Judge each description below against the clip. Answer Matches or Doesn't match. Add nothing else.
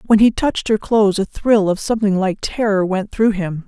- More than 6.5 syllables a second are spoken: Doesn't match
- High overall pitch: Matches